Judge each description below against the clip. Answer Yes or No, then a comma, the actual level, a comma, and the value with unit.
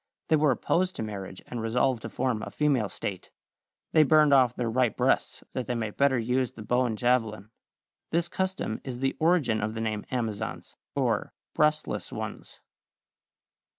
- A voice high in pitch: No, low, 125 Hz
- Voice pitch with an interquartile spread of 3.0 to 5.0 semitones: Yes, average, 4.4 semitones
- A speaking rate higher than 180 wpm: No, average, 170 wpm